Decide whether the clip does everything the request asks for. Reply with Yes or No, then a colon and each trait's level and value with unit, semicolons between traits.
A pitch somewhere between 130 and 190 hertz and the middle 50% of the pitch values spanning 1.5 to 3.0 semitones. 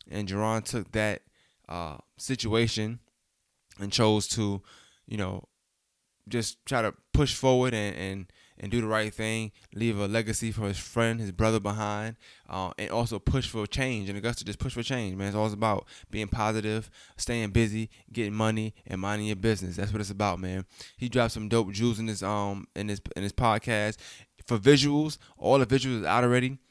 No: low, 110 Hz; narrow, 2.4 semitones